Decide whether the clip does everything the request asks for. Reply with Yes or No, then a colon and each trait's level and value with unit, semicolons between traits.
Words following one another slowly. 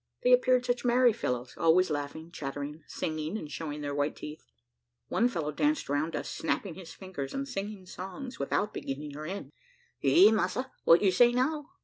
No: average, 175 wpm